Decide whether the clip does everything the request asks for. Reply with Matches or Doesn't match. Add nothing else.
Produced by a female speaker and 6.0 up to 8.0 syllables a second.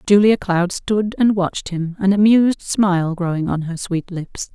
Doesn't match